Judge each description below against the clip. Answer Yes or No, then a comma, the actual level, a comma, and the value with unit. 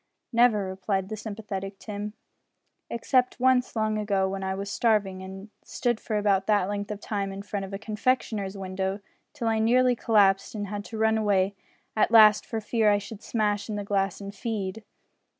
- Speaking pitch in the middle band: No, high, 205 Hz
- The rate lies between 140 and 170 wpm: No, average, 185 wpm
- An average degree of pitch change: No, narrow, 2.2 semitones